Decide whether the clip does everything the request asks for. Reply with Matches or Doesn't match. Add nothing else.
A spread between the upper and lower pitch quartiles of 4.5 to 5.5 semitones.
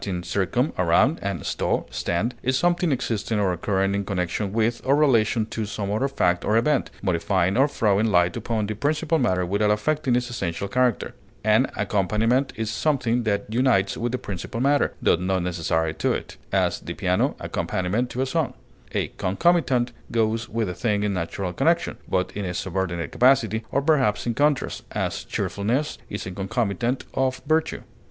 Matches